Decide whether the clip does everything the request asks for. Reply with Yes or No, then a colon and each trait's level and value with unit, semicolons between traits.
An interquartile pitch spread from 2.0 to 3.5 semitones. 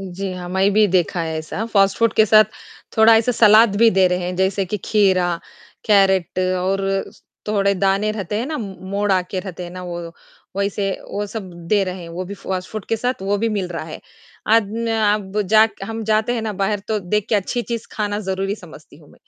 Yes: narrow, 2.6 semitones